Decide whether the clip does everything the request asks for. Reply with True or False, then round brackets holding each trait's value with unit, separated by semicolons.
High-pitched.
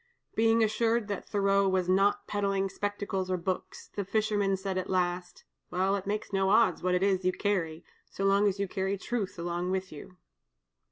True (195 Hz)